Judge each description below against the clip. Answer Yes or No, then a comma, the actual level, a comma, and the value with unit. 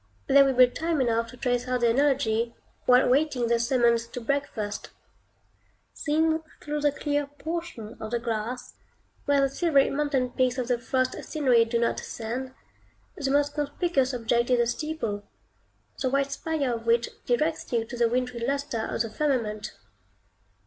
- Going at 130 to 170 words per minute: Yes, average, 165 wpm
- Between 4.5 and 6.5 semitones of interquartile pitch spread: No, average, 3.4 semitones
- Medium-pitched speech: No, very high, 255 Hz